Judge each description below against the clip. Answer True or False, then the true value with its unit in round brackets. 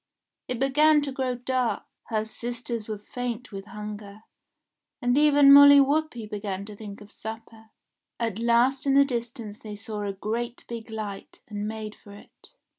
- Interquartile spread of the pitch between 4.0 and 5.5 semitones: False (3.3 semitones)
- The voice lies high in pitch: True (230 Hz)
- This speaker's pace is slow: False (165 wpm)